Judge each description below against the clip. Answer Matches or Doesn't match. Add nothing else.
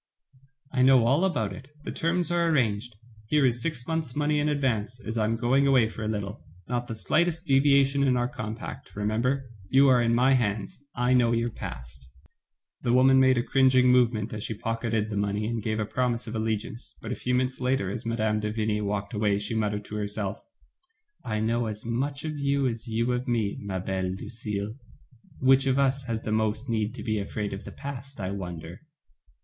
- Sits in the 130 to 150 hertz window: Doesn't match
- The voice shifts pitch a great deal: Doesn't match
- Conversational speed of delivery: Doesn't match